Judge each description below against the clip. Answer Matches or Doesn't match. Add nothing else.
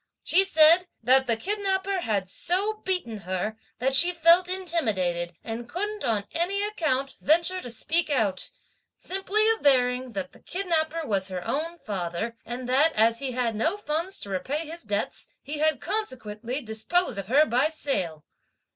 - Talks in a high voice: Matches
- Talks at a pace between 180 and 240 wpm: Doesn't match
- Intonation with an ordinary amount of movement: Doesn't match